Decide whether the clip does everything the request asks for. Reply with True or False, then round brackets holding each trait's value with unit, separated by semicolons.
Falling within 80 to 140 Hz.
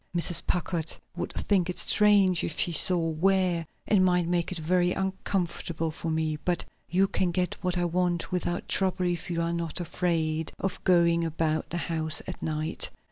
False (175 Hz)